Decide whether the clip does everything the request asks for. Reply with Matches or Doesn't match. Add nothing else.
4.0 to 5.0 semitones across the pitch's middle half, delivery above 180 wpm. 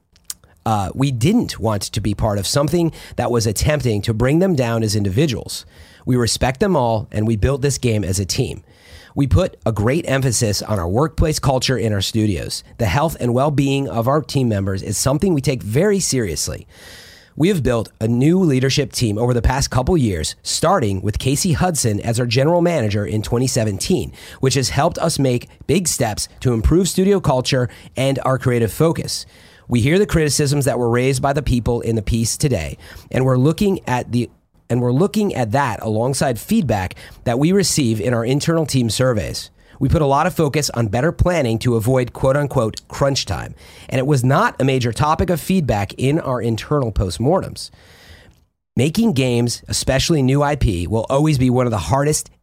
Matches